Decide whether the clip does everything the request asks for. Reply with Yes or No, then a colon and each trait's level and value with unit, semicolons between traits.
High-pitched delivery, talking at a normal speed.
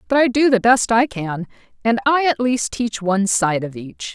No: high, 215 Hz; fast, 230 wpm